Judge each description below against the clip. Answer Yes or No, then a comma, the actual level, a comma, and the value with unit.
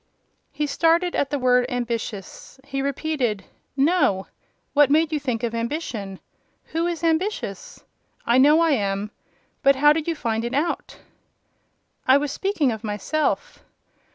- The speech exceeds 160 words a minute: No, average, 145 wpm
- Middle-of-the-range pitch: No, very high, 280 Hz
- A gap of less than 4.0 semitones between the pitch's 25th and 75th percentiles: No, average, 5.2 semitones